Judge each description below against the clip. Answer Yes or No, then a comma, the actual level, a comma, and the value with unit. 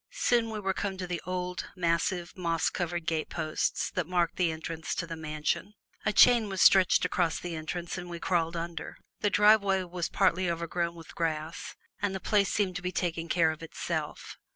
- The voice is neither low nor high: Yes, medium, 175 Hz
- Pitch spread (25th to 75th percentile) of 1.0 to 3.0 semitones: Yes, narrow, 2.4 semitones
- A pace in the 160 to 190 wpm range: Yes, average, 185 wpm